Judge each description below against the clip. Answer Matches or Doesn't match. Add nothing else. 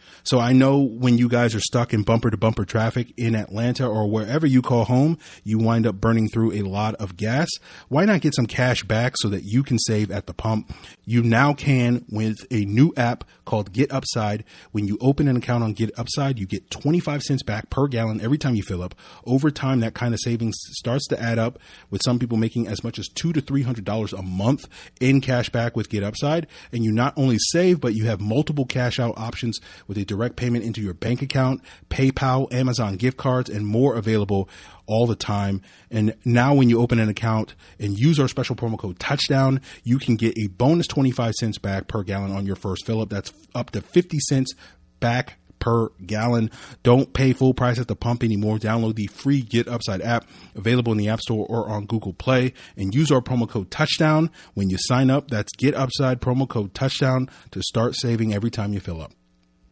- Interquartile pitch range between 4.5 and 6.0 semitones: Doesn't match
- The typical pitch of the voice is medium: Doesn't match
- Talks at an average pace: Doesn't match